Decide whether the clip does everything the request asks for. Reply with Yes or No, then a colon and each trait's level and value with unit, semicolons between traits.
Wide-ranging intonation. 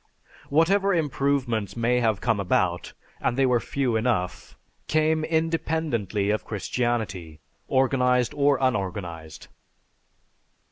Yes: wide, 5.7 semitones